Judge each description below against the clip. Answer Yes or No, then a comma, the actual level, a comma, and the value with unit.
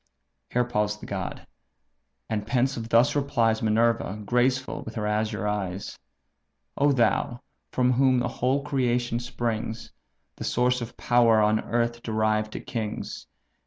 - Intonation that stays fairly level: Yes, narrow, 2.3 semitones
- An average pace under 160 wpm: Yes, slow, 135 wpm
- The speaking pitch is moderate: No, low, 115 Hz